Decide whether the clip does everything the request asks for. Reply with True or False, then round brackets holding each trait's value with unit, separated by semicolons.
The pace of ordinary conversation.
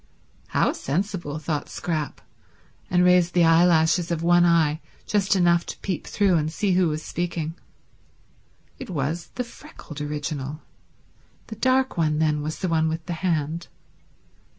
True (150 wpm)